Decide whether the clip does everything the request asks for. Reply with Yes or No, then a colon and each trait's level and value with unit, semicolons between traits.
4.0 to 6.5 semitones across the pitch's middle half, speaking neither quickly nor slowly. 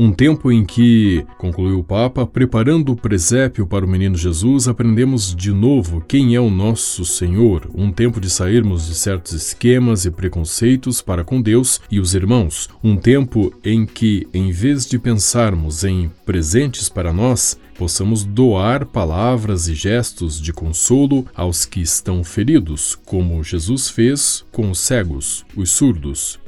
Yes: average, 5.3 semitones; average, 155 wpm